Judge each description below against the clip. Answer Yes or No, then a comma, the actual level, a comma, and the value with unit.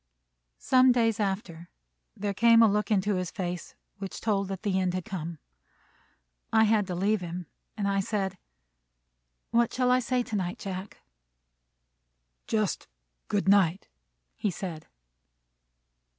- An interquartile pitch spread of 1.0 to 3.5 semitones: Yes, average, 3.0 semitones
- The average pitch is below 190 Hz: No, high, 200 Hz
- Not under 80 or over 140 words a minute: Yes, slow, 135 wpm